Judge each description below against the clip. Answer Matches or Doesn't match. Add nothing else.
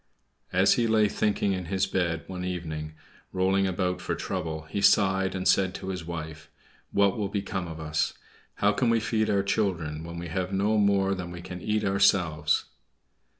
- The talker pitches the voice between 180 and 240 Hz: Doesn't match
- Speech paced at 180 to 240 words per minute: Matches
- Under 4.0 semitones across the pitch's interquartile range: Matches